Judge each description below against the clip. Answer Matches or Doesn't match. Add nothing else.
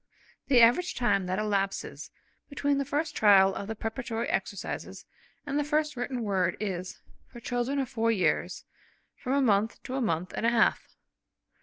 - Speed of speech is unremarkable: Matches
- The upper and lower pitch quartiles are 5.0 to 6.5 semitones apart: Matches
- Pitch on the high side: Matches